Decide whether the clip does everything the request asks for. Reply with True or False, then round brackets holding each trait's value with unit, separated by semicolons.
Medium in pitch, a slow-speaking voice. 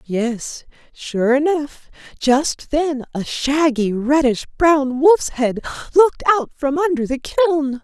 False (285 Hz; 130 wpm)